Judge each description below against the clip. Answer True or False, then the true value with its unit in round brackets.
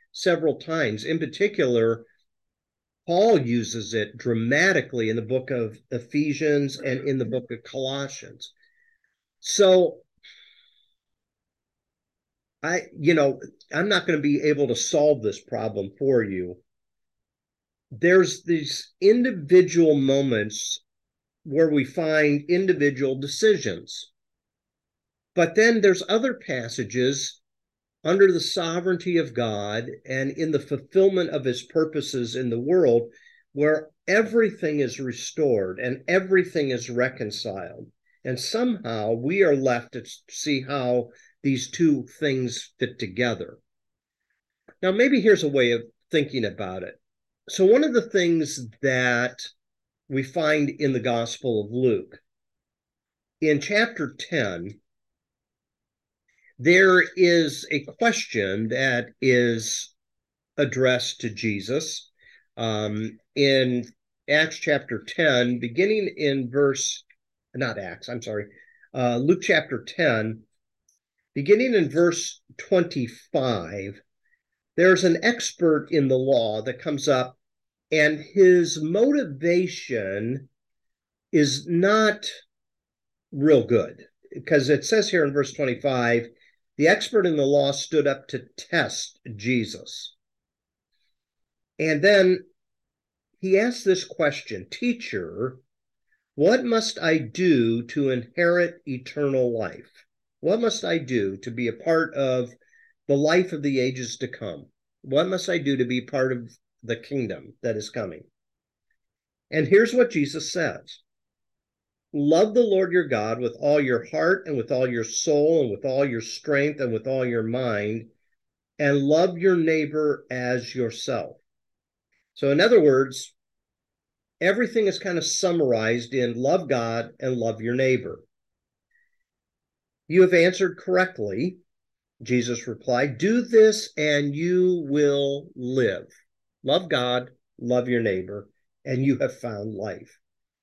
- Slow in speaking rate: True (125 wpm)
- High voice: False (140 Hz)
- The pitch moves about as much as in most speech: False (6.3 semitones)